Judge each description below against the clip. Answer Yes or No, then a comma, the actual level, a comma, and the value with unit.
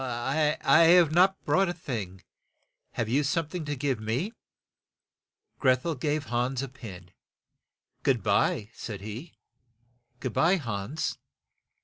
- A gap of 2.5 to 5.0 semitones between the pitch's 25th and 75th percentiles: No, wide, 5.5 semitones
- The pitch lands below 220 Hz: Yes, low, 135 Hz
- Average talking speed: No, slow, 130 wpm